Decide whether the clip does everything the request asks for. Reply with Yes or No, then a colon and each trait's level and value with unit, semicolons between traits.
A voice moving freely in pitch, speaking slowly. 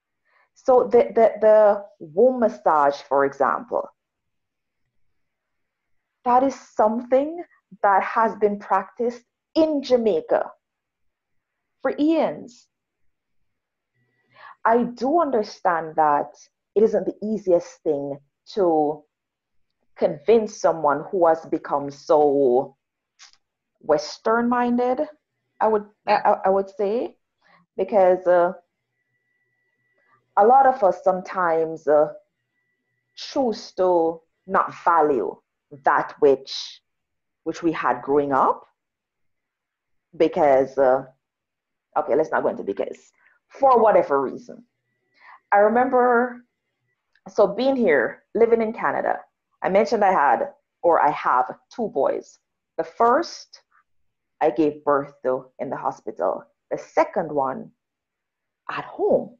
Yes: wide, 8.2 semitones; slow, 105 wpm